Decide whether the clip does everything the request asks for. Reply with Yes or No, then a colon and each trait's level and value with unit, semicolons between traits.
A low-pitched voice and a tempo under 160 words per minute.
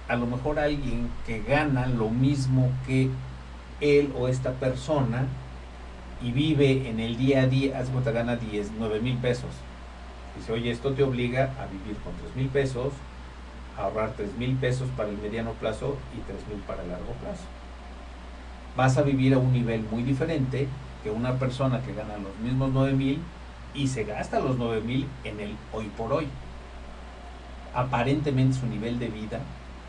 No: low, 120 Hz; average, 175 wpm